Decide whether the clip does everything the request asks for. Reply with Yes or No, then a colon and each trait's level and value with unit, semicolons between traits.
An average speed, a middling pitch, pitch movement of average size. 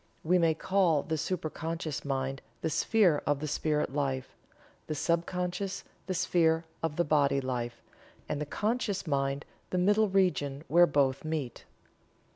Yes: average, 155 wpm; medium, 155 Hz; average, 4.1 semitones